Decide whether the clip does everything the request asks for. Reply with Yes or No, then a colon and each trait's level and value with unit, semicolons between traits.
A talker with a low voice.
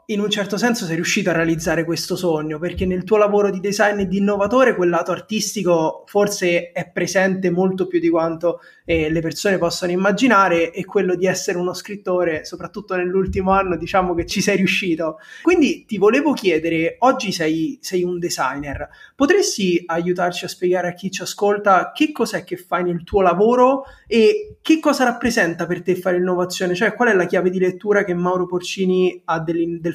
No: medium, 185 Hz